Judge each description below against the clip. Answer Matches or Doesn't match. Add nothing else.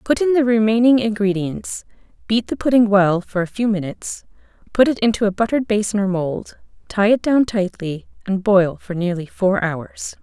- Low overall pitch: Doesn't match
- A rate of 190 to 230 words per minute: Doesn't match